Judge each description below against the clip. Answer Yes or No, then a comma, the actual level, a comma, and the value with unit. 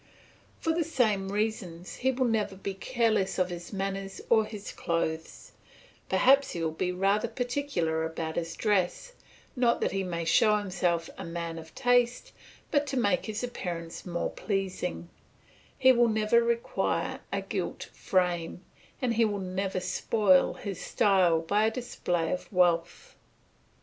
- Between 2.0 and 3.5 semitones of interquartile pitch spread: No, average, 4.9 semitones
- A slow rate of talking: No, average, 150 wpm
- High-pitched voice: Yes, high, 195 Hz